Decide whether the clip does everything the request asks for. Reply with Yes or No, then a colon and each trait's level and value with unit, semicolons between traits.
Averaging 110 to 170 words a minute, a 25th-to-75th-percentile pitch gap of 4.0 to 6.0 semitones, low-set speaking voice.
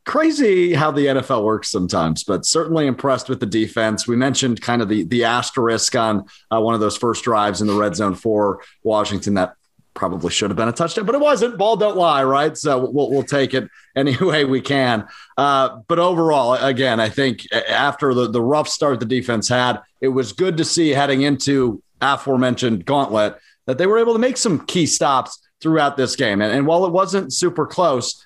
No: fast, 205 wpm; average, 5.3 semitones; low, 130 Hz